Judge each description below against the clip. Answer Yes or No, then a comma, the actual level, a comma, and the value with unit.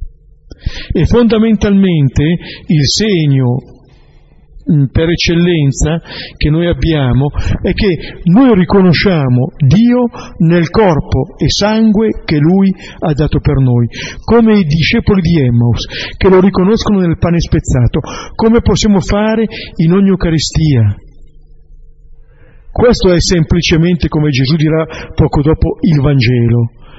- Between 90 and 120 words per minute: Yes, slow, 115 wpm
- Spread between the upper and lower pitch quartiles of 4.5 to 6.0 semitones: Yes, wide, 5.6 semitones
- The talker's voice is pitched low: No, medium, 165 Hz